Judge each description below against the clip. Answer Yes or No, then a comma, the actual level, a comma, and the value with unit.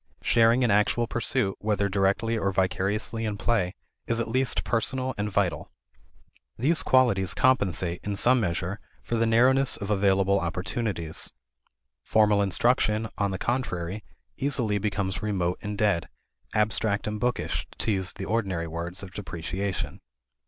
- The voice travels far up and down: No, average, 3.3 semitones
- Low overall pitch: Yes, low, 105 Hz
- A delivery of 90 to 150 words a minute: Yes, average, 140 wpm